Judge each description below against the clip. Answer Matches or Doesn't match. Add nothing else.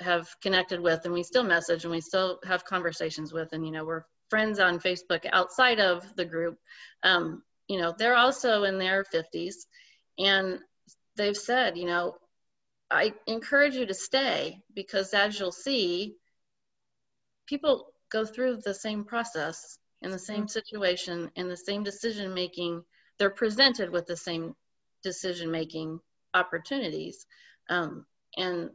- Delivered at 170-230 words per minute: Doesn't match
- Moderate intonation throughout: Matches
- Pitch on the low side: Doesn't match